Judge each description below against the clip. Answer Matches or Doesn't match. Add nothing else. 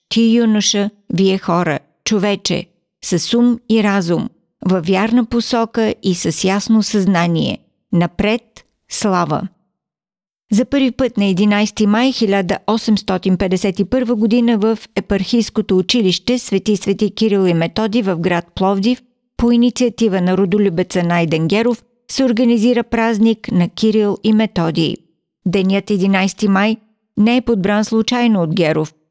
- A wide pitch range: Doesn't match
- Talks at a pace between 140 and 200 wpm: Doesn't match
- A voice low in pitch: Doesn't match